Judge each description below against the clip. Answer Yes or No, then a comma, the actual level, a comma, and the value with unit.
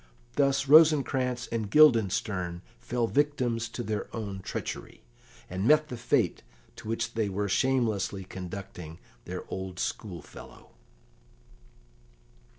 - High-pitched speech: No, low, 115 Hz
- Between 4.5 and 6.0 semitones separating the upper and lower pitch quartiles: Yes, average, 5.2 semitones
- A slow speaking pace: Yes, slow, 110 wpm